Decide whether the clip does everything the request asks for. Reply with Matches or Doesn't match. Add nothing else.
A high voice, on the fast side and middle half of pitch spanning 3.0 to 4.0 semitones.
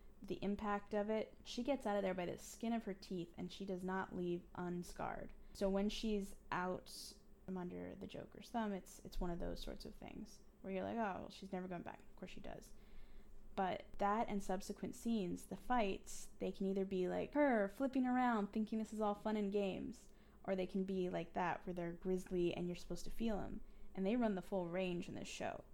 Doesn't match